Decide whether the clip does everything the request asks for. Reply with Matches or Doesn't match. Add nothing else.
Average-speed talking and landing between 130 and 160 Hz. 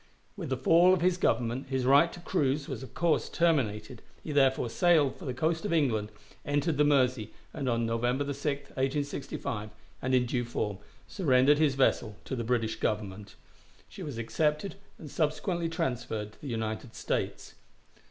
Matches